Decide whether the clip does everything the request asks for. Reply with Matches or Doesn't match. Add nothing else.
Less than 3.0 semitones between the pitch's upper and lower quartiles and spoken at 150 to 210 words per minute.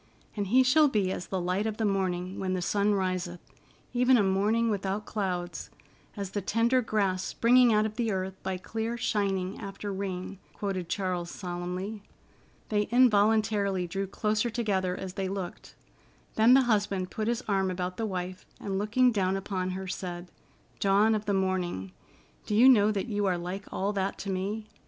Matches